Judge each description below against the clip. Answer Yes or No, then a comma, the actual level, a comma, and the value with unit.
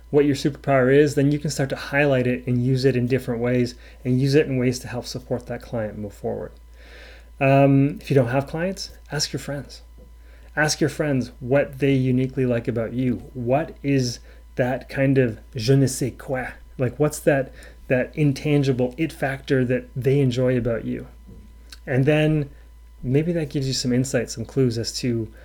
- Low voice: Yes, low, 130 Hz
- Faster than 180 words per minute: Yes, average, 190 wpm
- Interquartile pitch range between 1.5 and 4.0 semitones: Yes, narrow, 2.6 semitones